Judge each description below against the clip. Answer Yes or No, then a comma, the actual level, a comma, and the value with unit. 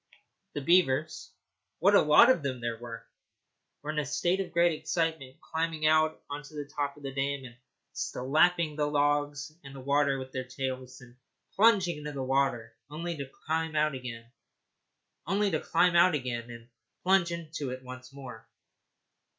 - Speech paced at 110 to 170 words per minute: Yes, average, 155 wpm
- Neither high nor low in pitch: Yes, medium, 145 Hz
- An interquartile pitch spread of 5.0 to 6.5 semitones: No, average, 3.7 semitones